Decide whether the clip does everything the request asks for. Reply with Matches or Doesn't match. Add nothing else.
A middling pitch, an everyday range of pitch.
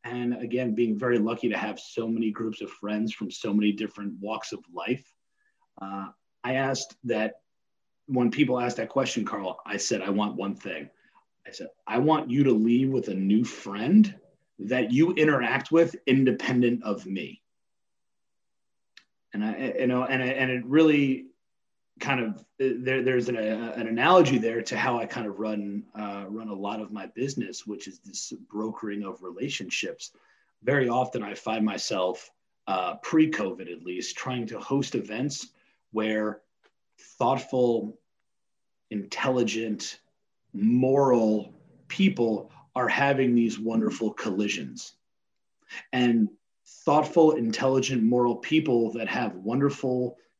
Doesn't match